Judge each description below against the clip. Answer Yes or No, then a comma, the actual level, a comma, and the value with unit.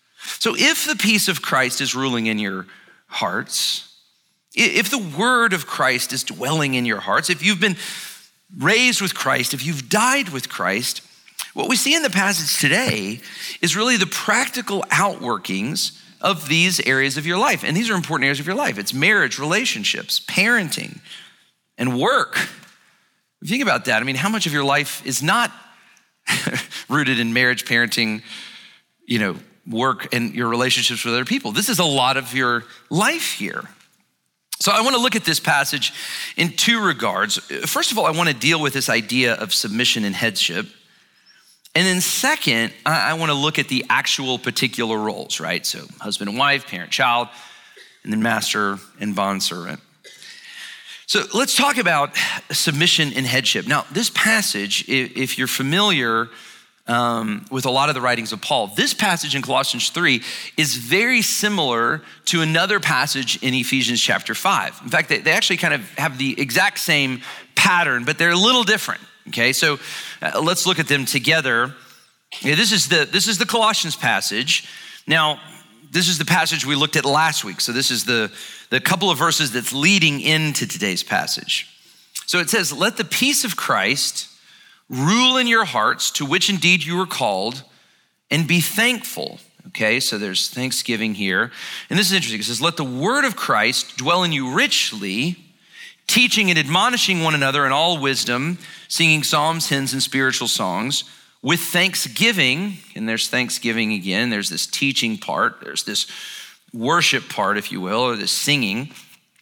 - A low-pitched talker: No, medium, 155 Hz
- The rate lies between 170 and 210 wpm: Yes, average, 175 wpm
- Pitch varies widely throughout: Yes, wide, 7.4 semitones